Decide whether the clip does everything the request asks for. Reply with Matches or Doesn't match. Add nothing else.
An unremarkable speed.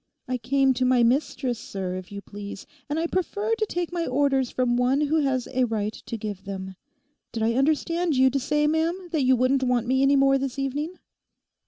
Doesn't match